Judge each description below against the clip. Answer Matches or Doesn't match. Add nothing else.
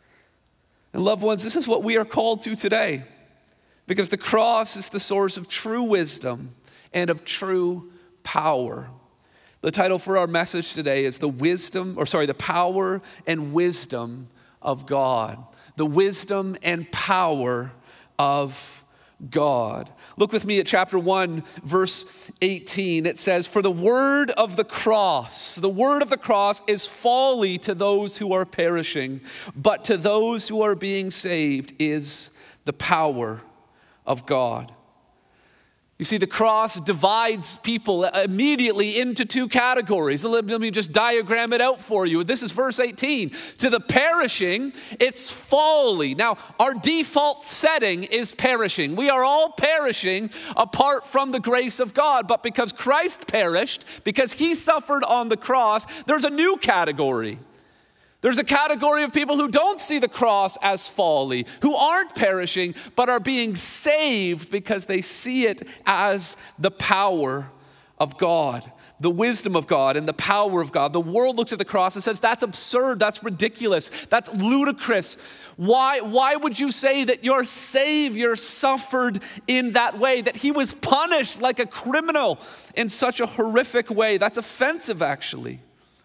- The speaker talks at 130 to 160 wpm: Matches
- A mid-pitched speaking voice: Doesn't match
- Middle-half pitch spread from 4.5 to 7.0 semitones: Matches